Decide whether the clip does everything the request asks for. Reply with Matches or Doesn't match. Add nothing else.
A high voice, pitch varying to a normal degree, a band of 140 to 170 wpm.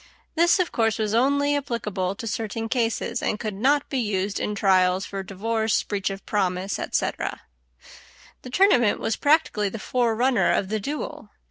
Matches